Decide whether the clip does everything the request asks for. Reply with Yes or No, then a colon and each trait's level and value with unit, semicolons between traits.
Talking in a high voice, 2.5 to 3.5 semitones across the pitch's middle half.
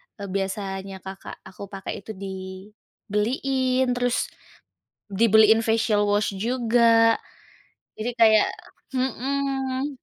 No: high, 220 Hz; average, 3.9 semitones